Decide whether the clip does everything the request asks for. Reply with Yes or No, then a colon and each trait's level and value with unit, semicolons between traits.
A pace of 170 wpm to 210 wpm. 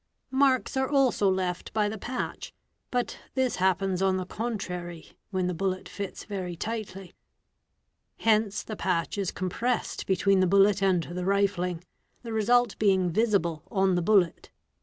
No: average, 155 wpm